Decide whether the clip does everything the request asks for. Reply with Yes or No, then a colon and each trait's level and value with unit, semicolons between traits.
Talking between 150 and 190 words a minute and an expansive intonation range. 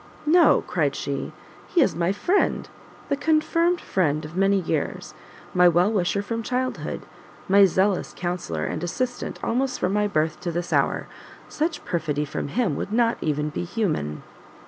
Yes: average, 160 wpm; wide, 7.1 semitones